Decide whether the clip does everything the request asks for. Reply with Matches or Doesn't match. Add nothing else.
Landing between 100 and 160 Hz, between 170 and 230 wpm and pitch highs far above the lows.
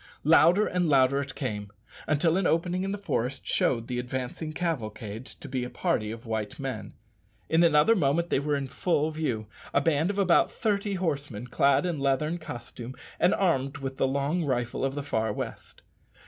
Doesn't match